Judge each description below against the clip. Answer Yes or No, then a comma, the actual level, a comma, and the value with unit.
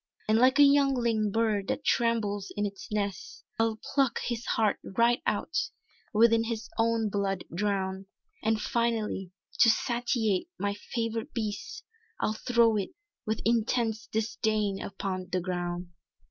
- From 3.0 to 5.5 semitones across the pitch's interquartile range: No, narrow, 2.5 semitones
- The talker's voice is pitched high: Yes, high, 220 Hz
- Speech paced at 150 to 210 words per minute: No, slow, 135 wpm